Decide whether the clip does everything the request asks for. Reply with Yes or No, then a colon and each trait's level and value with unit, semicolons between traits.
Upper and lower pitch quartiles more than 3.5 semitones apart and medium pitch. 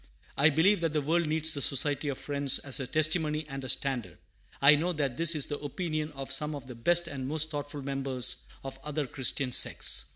No: narrow, 2.4 semitones; medium, 145 Hz